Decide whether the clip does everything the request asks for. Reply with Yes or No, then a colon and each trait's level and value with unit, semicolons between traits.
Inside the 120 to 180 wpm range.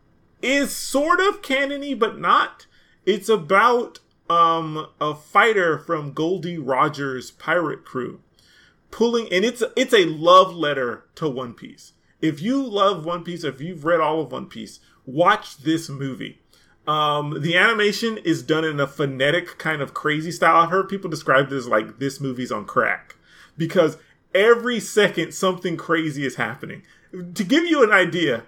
Yes: average, 160 wpm